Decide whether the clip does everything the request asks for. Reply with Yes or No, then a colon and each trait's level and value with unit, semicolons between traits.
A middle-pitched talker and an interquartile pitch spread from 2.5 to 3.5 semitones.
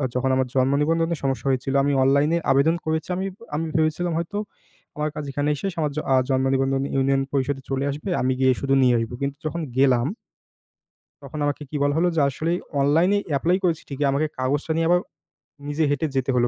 Yes: medium, 145 Hz; average, 3.2 semitones